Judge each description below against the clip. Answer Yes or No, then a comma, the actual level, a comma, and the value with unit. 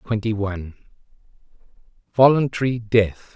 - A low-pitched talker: Yes, low, 110 Hz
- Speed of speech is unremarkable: No, slow, 70 wpm